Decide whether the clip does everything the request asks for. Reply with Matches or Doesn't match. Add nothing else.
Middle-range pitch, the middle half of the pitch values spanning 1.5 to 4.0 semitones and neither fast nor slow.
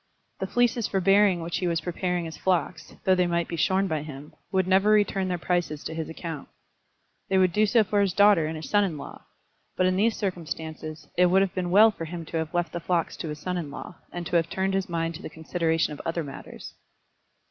Doesn't match